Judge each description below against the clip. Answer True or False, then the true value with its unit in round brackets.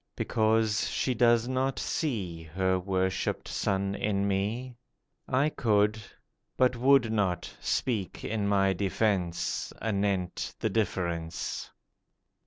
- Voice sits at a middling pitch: False (105 Hz)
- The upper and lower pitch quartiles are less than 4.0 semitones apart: True (3.4 semitones)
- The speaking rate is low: True (105 wpm)